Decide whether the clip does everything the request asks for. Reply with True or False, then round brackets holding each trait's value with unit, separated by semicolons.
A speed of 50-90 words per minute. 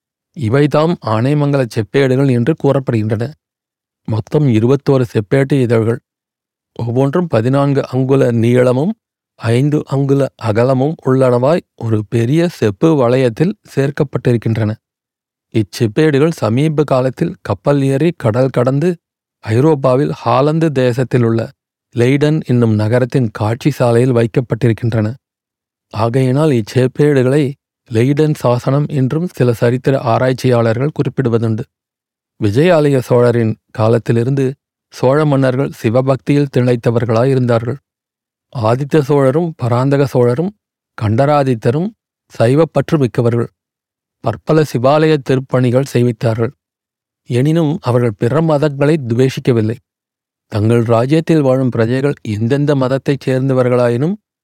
True (85 wpm)